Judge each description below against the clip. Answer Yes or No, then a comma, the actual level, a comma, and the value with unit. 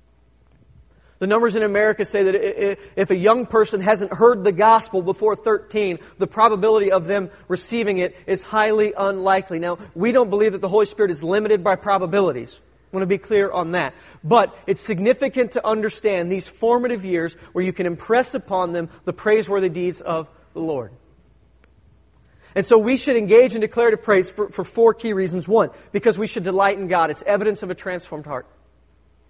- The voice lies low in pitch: No, high, 200 Hz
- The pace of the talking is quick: No, average, 185 wpm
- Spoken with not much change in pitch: No, average, 3.2 semitones